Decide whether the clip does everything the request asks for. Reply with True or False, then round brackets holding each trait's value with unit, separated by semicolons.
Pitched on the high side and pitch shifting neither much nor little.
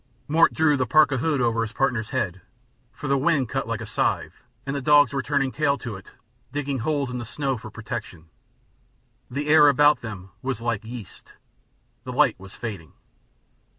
False (130 Hz; 4.2 semitones)